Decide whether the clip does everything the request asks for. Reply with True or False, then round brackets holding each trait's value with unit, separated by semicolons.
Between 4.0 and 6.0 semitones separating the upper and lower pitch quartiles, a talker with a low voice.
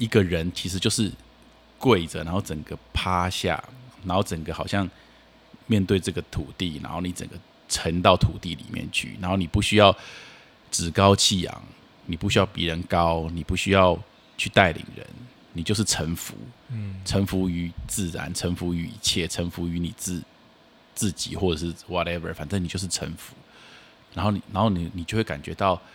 False (3.0 semitones; 90 Hz)